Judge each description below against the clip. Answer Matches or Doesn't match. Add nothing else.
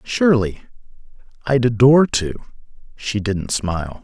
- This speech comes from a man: Matches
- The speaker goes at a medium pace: Doesn't match